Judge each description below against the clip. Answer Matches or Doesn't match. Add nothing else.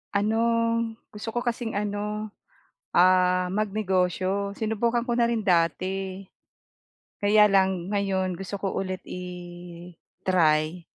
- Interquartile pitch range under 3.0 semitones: Matches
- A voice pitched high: Matches